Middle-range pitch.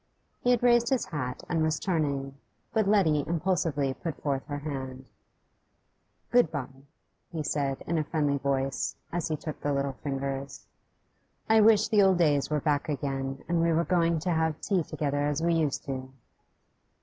Yes: medium, 150 Hz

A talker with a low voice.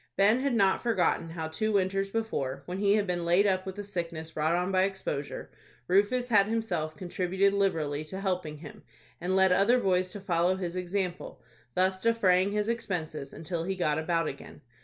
No: medium, 185 Hz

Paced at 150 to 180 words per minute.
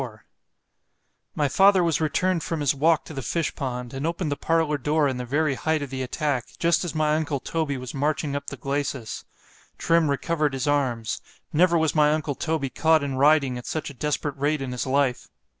No: average, 195 wpm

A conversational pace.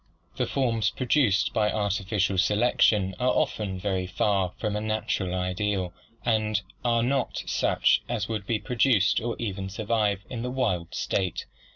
Yes: average, 150 wpm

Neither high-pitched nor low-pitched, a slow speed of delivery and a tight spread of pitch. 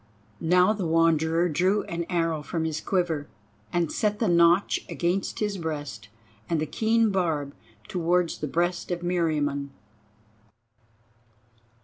Yes: medium, 170 Hz; slow, 125 wpm; narrow, 2.2 semitones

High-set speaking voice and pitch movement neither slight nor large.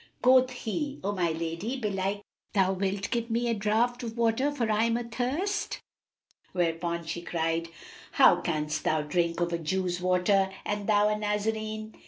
Yes: high, 205 Hz; average, 4.9 semitones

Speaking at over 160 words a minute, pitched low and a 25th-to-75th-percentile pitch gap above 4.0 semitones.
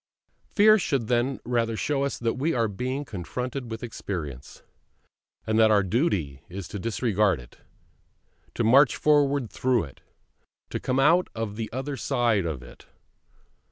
No: average, 155 wpm; low, 115 Hz; average, 4.8 semitones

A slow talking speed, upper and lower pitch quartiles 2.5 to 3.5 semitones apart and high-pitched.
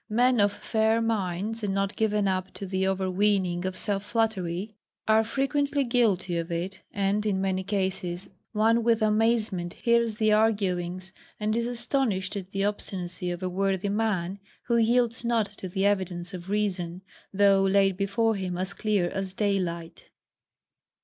No: average, 155 wpm; average, 2.9 semitones; high, 200 Hz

